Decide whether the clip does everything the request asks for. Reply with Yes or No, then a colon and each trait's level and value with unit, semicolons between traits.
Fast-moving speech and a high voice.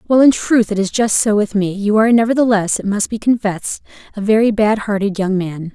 Yes: fast, 230 wpm; high, 210 Hz